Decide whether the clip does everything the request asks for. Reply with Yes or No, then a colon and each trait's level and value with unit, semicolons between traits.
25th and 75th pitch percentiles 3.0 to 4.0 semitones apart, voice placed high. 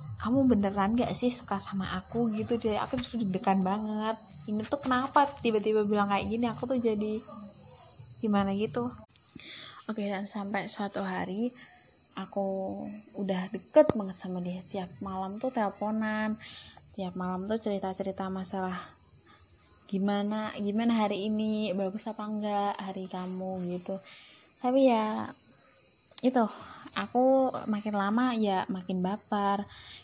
No: narrow, 2.5 semitones; high, 205 Hz